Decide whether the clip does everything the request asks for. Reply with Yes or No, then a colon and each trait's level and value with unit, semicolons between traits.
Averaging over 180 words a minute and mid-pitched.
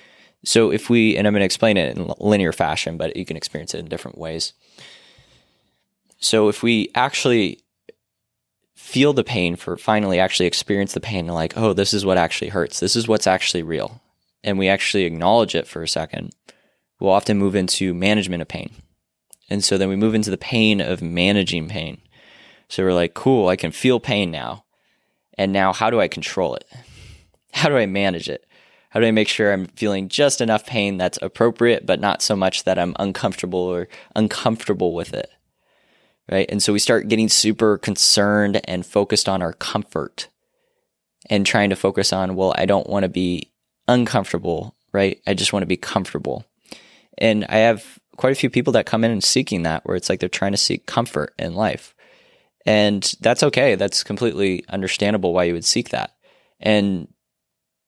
No: average, 190 wpm; low, 100 Hz